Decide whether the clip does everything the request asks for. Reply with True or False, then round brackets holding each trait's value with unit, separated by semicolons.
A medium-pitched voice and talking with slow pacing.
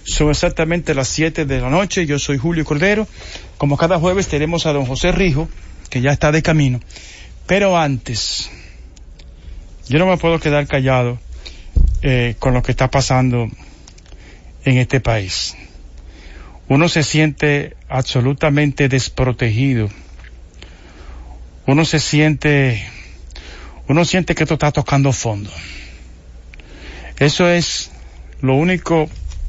False (130 Hz; 120 wpm)